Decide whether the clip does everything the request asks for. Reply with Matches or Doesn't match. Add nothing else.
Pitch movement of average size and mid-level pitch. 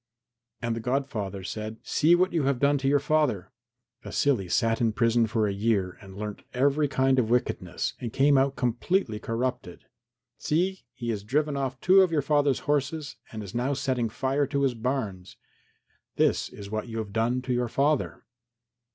Doesn't match